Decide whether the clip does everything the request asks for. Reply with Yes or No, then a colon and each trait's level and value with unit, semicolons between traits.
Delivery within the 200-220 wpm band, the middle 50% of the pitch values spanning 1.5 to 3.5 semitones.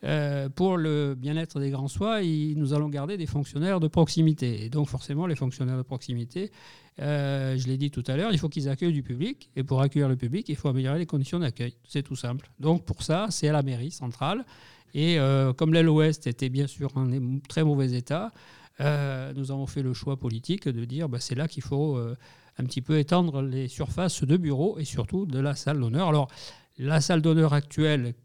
Yes: average, 215 wpm; average, 3.1 semitones